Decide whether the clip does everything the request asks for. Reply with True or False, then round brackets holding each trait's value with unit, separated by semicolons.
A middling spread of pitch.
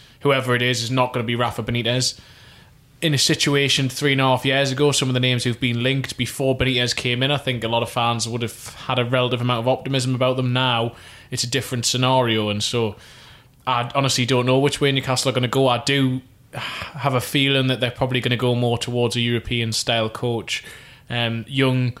False (1.8 semitones)